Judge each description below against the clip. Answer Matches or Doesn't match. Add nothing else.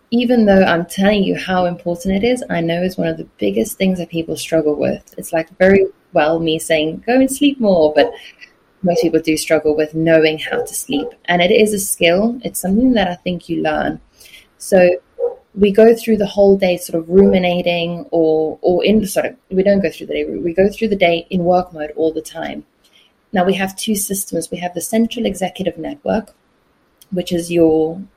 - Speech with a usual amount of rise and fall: Matches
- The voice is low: Doesn't match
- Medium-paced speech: Doesn't match